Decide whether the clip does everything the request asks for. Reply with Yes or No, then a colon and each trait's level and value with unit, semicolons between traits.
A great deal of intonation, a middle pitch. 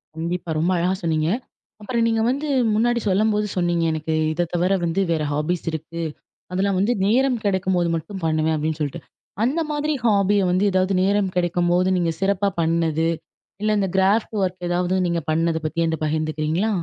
No: average, 3.6 semitones; medium, 180 Hz